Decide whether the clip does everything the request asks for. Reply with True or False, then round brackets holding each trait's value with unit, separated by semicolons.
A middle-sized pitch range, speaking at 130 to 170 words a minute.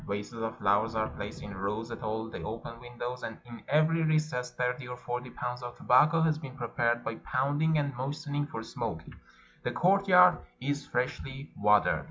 False (4.3 semitones; 185 wpm)